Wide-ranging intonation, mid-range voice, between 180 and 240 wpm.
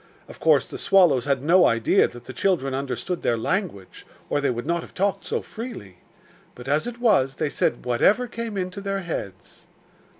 Yes: wide, 7.8 semitones; medium, 155 Hz; average, 190 wpm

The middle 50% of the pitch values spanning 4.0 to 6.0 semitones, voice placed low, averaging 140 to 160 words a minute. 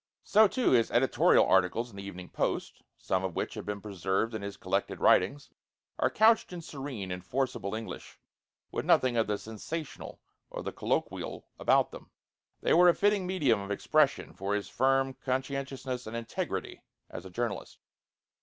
No: wide, 5.5 semitones; low, 120 Hz; average, 170 wpm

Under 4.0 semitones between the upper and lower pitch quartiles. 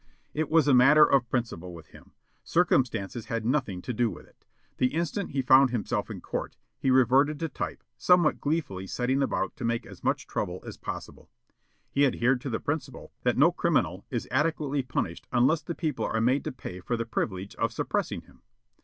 No: average, 4.4 semitones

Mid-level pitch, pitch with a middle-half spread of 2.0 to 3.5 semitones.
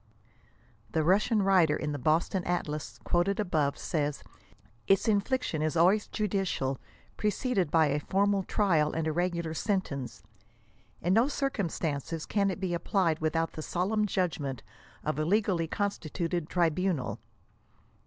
No: medium, 175 Hz; average, 4.3 semitones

